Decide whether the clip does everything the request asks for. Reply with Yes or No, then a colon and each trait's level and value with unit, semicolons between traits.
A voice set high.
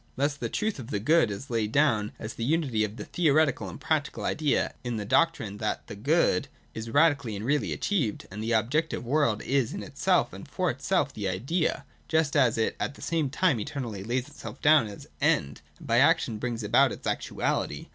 No: low, 130 Hz